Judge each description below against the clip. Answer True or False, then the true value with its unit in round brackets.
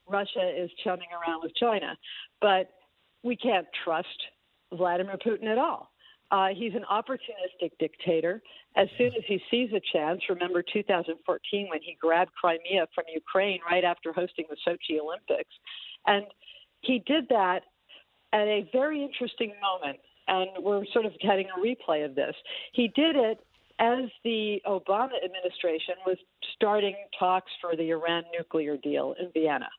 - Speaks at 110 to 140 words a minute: False (150 wpm)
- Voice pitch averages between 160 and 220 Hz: True (190 Hz)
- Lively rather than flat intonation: False (4.5 semitones)